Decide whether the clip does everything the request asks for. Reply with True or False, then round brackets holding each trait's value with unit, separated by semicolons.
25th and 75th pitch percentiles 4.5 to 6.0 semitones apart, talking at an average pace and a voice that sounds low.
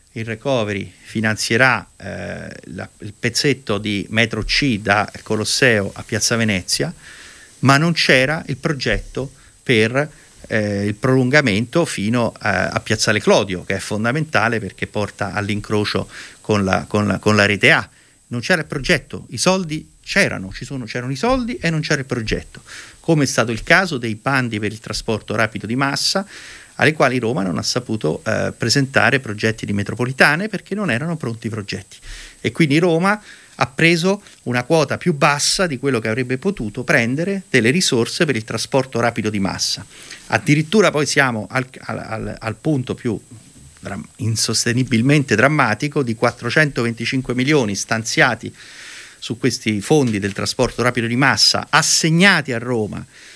True (5.3 semitones; 155 wpm; 120 Hz)